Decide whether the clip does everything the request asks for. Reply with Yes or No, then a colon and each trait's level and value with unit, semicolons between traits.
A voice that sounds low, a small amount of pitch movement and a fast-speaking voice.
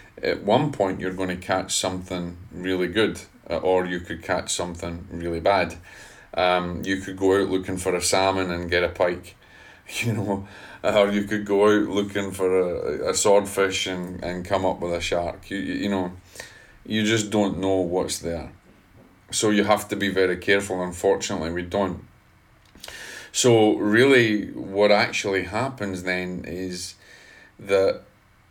No: very low, 95 Hz; narrow, 2.0 semitones; average, 160 wpm